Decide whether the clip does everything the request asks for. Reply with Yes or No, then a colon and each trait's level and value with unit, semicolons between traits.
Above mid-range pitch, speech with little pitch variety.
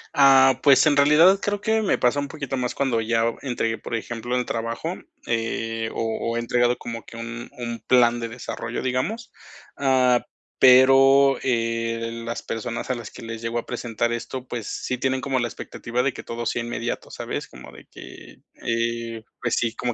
No: low, 120 Hz; narrow, 2.3 semitones